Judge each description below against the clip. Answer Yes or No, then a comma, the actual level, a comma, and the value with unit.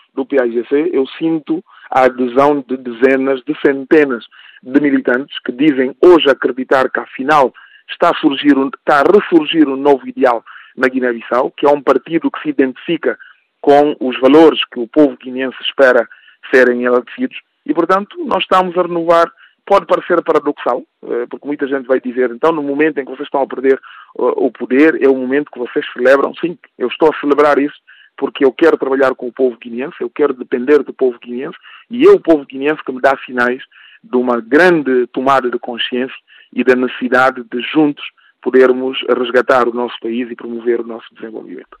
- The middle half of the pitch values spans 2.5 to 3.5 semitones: No, average, 4.1 semitones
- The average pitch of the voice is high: No, low, 135 Hz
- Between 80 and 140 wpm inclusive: No, fast, 185 wpm